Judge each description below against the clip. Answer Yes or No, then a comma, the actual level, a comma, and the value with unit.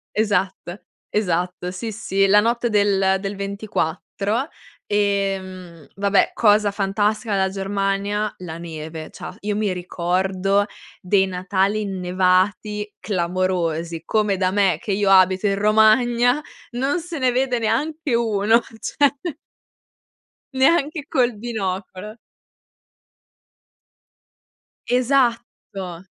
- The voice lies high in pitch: Yes, high, 200 Hz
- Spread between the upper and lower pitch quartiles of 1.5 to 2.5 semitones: No, average, 2.9 semitones